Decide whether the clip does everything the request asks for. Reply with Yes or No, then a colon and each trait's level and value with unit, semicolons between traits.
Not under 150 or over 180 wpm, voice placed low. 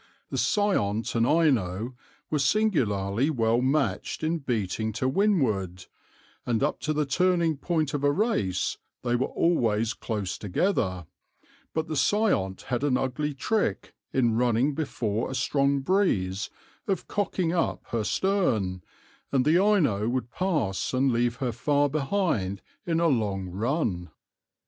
No: average, 140 wpm; low, 130 Hz